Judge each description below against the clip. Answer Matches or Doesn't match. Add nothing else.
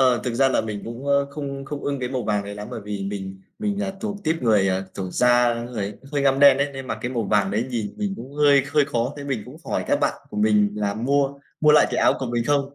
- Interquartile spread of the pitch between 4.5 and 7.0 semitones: Matches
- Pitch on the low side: Matches